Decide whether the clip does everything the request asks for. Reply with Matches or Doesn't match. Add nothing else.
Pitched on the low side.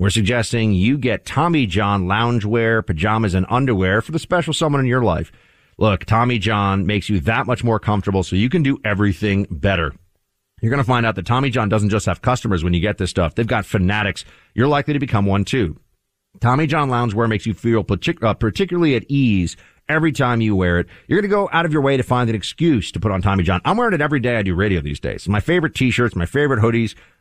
Matches